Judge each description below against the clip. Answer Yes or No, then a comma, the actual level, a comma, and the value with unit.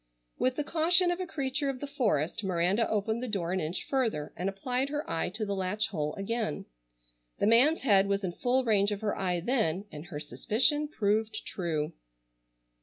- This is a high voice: Yes, high, 215 Hz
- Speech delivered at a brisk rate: No, average, 190 wpm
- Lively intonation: Yes, wide, 5.9 semitones